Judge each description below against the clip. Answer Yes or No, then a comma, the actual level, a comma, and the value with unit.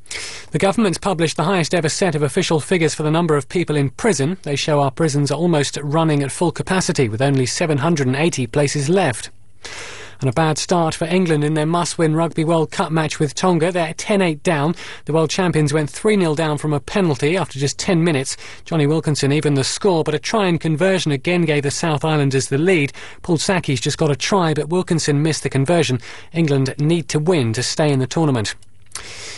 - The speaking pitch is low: No, medium, 155 Hz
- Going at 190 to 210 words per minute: Yes, fast, 205 wpm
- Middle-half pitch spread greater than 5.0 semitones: No, average, 3.3 semitones